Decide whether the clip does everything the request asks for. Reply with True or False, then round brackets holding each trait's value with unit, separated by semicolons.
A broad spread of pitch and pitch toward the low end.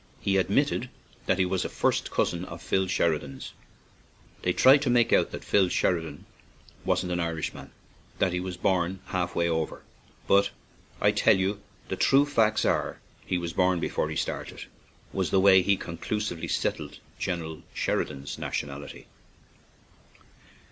False (2.5 semitones; 90 Hz)